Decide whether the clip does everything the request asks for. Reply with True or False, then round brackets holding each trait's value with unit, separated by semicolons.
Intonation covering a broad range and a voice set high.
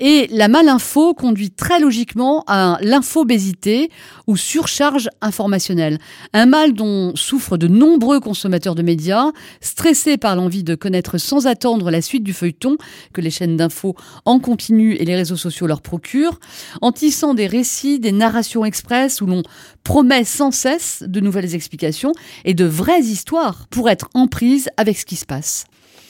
True (7.2 semitones; 220 Hz)